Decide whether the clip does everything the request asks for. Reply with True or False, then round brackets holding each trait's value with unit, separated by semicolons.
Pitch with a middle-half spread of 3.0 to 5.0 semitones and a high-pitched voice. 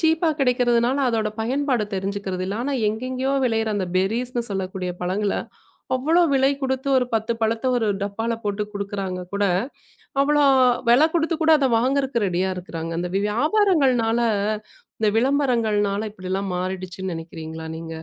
False (5.4 semitones; 225 Hz)